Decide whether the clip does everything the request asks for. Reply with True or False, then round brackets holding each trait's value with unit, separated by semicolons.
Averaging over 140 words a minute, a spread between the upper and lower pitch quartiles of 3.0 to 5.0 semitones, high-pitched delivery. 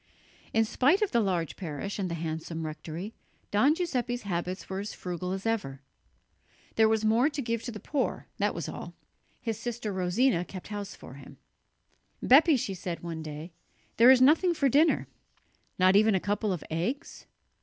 False (175 wpm; 5.6 semitones; 205 Hz)